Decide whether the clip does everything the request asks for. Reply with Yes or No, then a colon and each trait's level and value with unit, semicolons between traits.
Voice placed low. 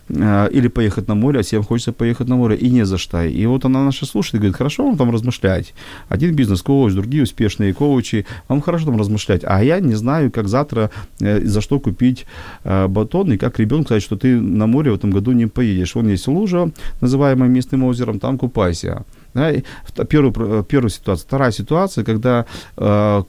Yes: low, 115 Hz